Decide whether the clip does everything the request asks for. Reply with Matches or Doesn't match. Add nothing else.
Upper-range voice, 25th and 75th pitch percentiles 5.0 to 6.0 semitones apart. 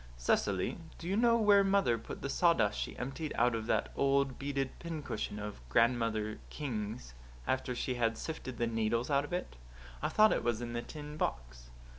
Doesn't match